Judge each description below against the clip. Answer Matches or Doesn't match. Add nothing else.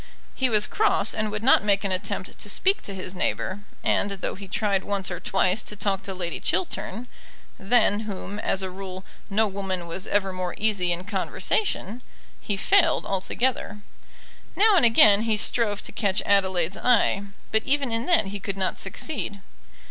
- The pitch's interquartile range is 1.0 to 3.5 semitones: Matches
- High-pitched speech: Matches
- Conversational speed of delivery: Matches